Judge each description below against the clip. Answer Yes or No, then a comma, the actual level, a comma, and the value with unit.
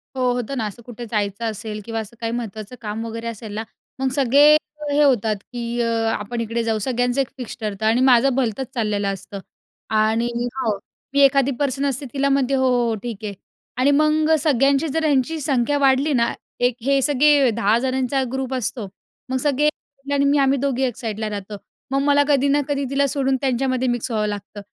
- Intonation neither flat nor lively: Yes, average, 3.5 semitones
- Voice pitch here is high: Yes, very high, 250 Hz